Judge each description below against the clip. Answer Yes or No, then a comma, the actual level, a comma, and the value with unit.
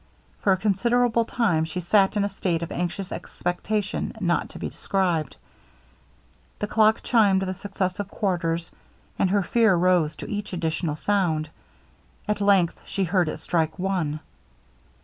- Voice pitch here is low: No, high, 190 Hz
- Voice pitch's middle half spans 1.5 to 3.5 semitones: Yes, average, 3.1 semitones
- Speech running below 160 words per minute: Yes, average, 150 wpm